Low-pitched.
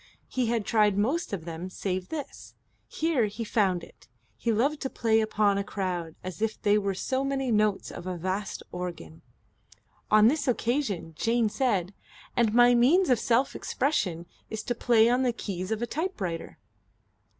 No: high, 220 Hz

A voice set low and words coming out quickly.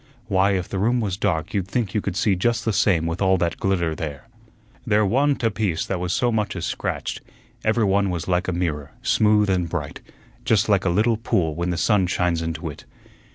Yes: very low, 95 Hz; fast, 220 wpm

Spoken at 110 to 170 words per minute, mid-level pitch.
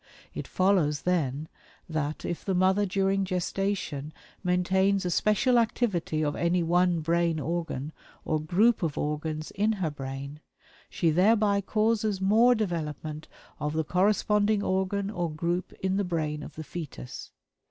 Yes: average, 140 wpm; medium, 180 Hz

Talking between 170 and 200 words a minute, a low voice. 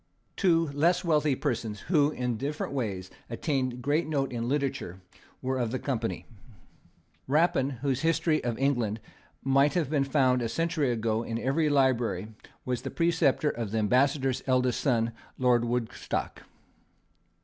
No: average, 145 wpm; low, 130 Hz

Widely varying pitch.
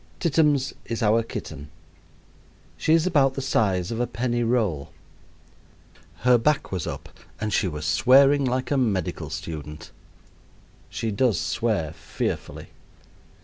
Yes: wide, 5.8 semitones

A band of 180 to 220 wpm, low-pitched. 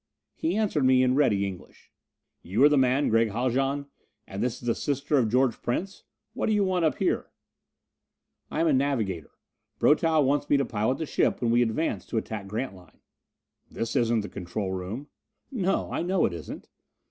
Yes: average, 190 wpm; low, 130 Hz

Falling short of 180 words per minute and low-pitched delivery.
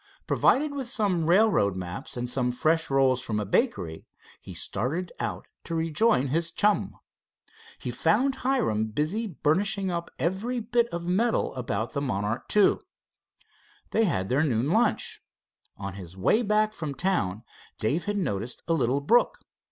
No: average, 150 wpm; medium, 160 Hz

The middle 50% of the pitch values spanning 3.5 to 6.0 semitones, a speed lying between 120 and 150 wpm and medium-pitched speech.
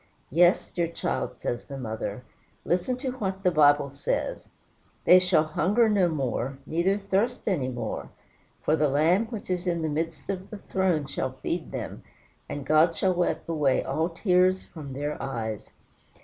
No: average, 4.6 semitones; average, 165 wpm; medium, 165 Hz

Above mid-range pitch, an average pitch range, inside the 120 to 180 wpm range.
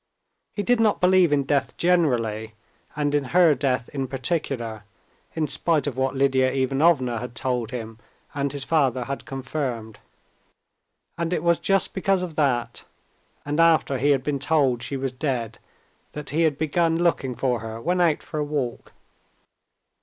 No: medium, 140 Hz; average, 4.2 semitones; average, 165 wpm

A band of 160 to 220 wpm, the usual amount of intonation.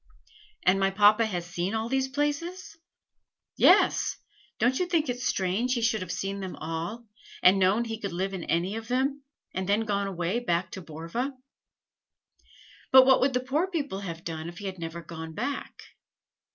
No: average, 180 wpm; wide, 6.1 semitones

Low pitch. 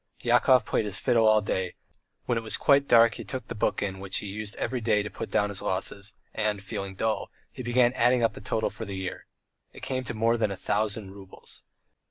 Yes: low, 110 Hz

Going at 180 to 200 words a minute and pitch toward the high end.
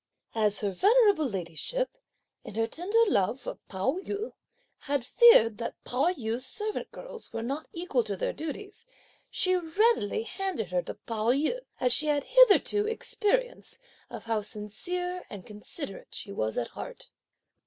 No: average, 155 wpm; very high, 290 Hz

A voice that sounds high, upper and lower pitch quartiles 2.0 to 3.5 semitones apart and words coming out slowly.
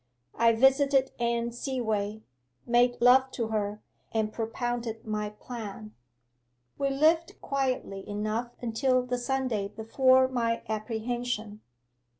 Yes: high, 235 Hz; average, 3.0 semitones; slow, 110 wpm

